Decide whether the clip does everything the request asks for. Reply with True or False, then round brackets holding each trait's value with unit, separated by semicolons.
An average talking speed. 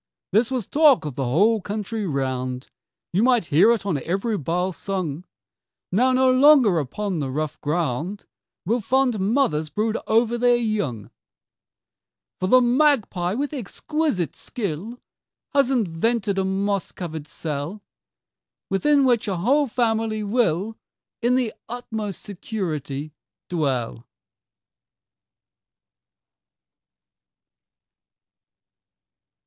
False (110 wpm)